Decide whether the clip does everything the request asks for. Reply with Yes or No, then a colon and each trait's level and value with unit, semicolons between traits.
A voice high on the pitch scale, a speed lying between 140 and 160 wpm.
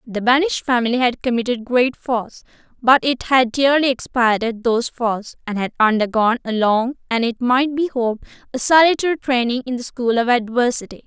No: high, 245 Hz; average, 175 wpm